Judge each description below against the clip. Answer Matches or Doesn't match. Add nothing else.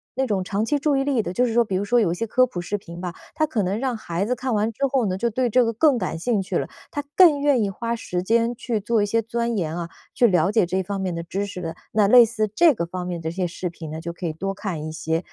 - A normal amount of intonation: Matches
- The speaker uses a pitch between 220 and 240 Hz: Doesn't match